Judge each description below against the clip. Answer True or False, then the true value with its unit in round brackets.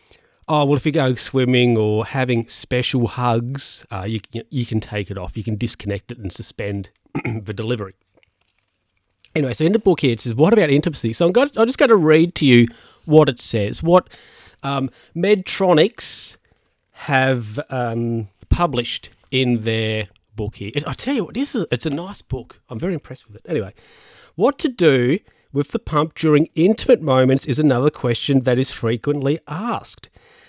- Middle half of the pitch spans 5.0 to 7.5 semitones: True (5.5 semitones)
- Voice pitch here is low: True (130 Hz)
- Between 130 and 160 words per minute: False (185 wpm)